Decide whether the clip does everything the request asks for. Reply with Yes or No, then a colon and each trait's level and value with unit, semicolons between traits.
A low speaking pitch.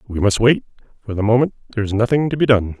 Yes: low, 115 Hz